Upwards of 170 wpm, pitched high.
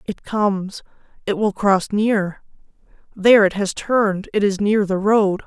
No: average, 145 wpm; high, 200 Hz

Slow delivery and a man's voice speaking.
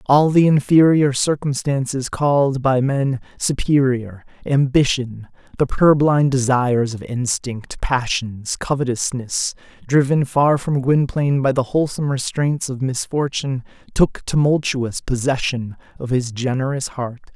Yes: slow, 115 wpm; male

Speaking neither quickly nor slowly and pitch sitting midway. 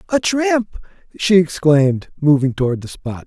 Yes: average, 145 wpm; medium, 165 Hz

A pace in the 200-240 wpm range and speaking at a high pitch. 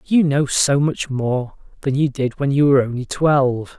No: fast, 205 wpm; medium, 140 Hz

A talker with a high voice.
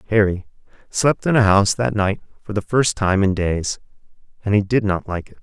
No: low, 105 Hz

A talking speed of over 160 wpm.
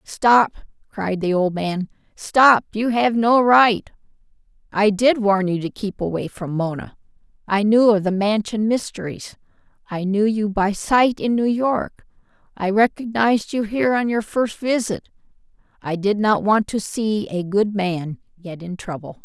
No: average, 150 wpm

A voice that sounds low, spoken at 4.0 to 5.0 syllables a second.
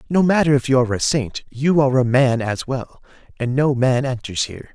No: low, 130 Hz; 5.6 syllables/s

